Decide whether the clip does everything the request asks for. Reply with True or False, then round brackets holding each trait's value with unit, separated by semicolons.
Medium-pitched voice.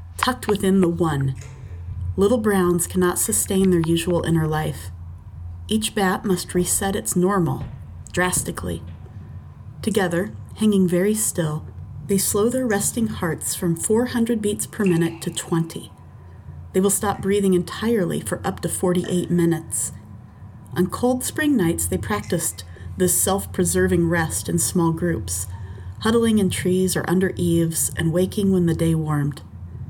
True (170 Hz)